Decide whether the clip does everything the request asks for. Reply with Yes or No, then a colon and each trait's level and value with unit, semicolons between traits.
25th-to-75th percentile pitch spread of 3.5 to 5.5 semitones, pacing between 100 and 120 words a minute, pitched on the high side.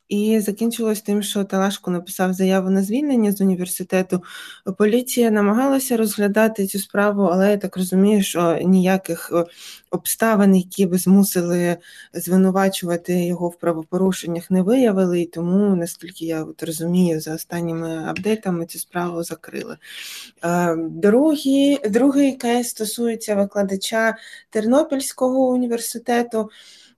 Yes: average, 4.0 semitones; average, 110 wpm; high, 195 Hz